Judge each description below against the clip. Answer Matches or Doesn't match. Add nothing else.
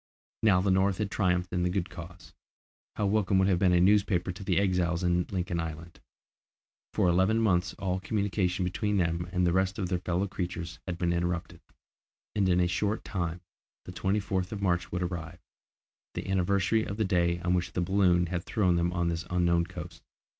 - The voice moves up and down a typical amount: Doesn't match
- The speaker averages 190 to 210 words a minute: Matches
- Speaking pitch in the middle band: Doesn't match